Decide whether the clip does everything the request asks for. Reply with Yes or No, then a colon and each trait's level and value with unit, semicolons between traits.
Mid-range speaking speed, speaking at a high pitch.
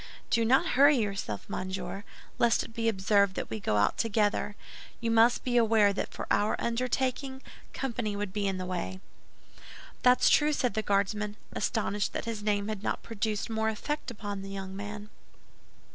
Yes: average, 175 wpm; high, 210 Hz